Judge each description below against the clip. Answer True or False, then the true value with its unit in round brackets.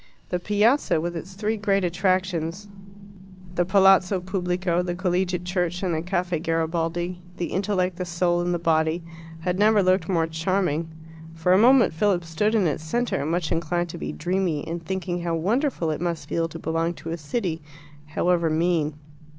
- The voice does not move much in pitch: True (2.3 semitones)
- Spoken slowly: False (175 wpm)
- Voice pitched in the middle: True (175 Hz)